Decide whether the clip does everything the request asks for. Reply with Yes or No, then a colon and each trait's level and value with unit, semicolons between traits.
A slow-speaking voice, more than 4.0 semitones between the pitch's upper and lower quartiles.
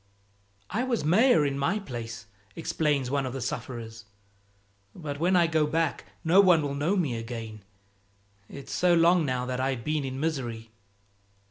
No: average, 160 wpm; average, 5.1 semitones